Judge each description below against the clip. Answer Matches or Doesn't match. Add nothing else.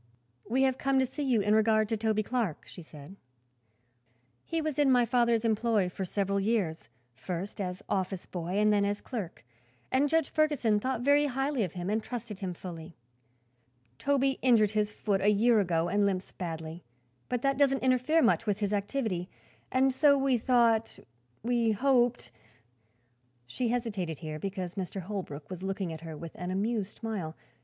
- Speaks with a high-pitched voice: Matches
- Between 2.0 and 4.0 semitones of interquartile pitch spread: Doesn't match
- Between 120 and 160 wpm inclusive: Doesn't match